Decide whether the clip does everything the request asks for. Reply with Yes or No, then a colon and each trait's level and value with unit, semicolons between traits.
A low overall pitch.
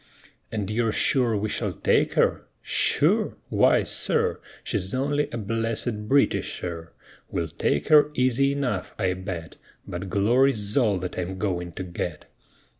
Yes: low, 105 Hz